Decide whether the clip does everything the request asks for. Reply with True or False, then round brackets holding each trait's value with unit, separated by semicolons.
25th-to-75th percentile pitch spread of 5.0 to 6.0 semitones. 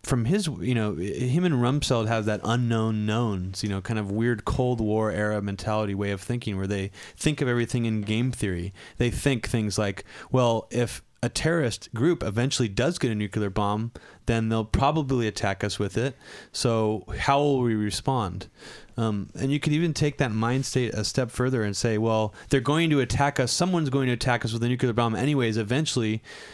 False (3.5 semitones)